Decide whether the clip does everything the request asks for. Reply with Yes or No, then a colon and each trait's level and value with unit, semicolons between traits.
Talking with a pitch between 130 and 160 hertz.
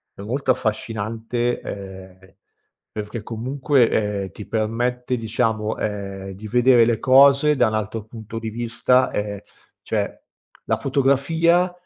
No: low, 115 Hz